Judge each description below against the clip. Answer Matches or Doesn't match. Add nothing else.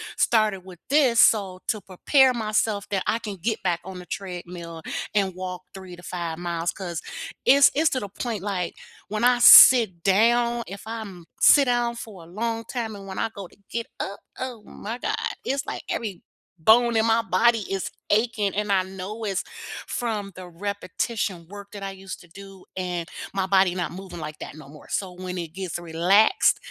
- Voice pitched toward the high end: Matches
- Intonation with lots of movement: Doesn't match